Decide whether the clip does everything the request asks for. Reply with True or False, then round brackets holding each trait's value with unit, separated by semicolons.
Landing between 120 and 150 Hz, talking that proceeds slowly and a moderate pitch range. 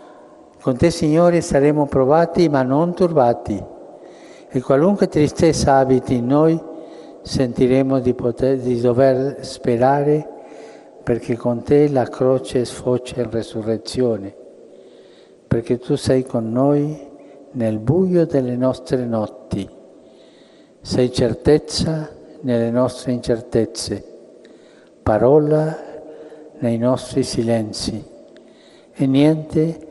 True (135 Hz; 100 wpm; 3.8 semitones)